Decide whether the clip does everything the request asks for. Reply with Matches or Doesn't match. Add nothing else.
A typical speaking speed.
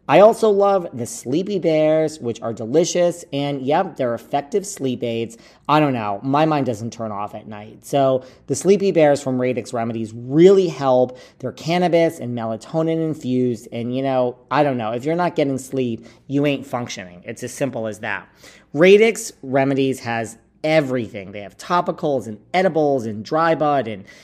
Matches